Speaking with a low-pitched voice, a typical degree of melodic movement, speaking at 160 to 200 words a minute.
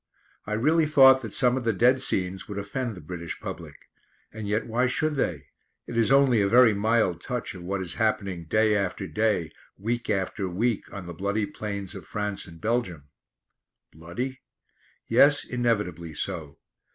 Yes: low, 105 Hz; average, 4.9 semitones; average, 170 wpm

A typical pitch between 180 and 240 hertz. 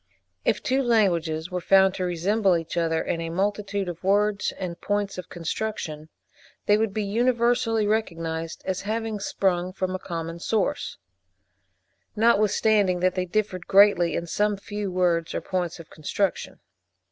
Yes: high, 190 Hz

